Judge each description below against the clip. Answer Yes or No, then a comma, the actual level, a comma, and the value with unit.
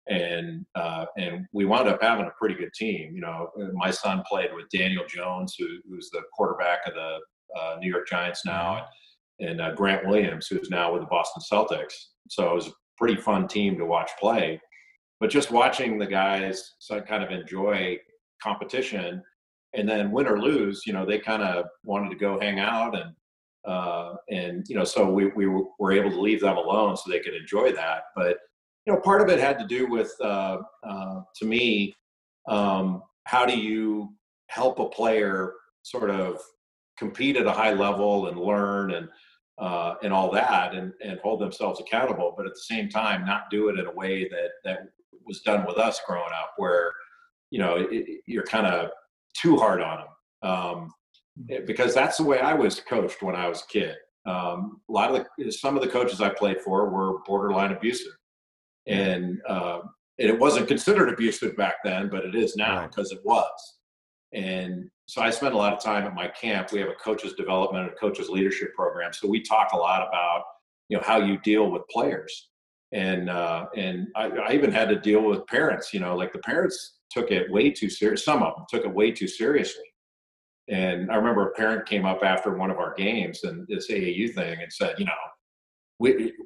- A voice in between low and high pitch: No, low, 100 Hz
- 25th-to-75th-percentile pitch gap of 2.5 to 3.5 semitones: No, average, 4.8 semitones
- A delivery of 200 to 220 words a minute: Yes, fast, 205 wpm